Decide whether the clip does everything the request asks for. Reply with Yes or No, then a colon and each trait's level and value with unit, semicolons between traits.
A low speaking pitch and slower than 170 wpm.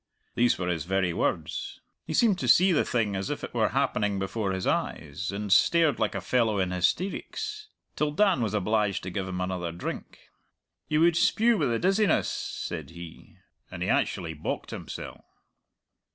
No: low, 105 Hz; average, 180 wpm